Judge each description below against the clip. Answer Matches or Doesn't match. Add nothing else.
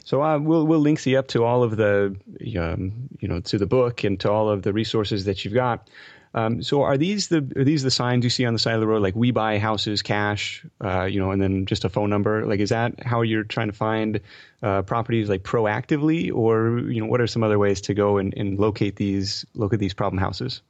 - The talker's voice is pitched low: Matches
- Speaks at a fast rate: Matches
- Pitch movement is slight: Doesn't match